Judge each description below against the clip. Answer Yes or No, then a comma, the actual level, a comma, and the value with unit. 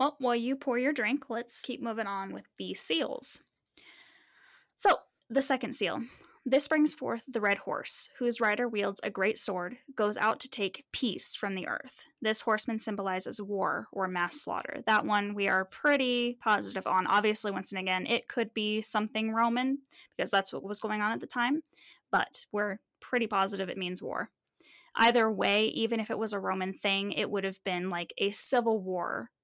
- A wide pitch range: No, average, 3.9 semitones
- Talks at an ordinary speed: Yes, average, 190 wpm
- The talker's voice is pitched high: Yes, high, 220 Hz